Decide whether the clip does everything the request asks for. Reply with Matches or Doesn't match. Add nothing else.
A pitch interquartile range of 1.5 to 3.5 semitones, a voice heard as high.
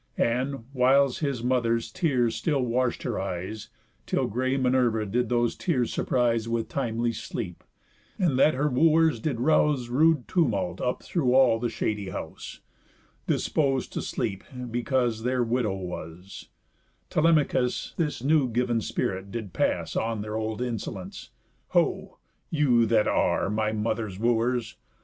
Doesn't match